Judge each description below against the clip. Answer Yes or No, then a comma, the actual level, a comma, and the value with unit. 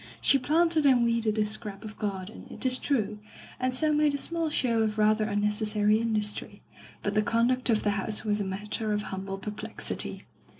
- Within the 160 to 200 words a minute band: Yes, average, 195 wpm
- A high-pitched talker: Yes, high, 215 Hz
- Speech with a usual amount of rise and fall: Yes, average, 3.3 semitones